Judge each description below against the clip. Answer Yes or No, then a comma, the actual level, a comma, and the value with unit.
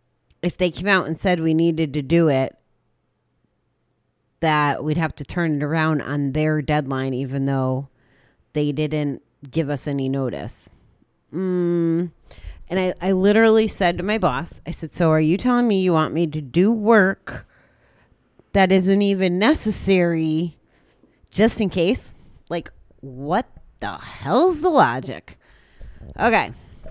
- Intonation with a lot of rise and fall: No, average, 4.1 semitones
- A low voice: No, medium, 165 Hz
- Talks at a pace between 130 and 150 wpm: Yes, average, 145 wpm